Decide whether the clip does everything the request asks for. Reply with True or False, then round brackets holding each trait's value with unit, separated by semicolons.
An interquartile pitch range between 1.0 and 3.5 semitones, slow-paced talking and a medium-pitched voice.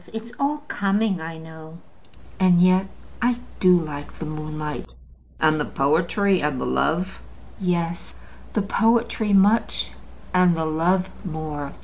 False (4.0 semitones; 130 wpm; 175 Hz)